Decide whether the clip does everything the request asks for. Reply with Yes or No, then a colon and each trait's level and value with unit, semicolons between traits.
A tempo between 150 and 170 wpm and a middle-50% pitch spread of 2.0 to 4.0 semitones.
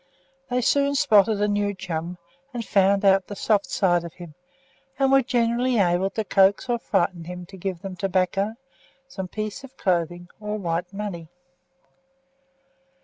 Yes: average, 155 wpm; average, 3.3 semitones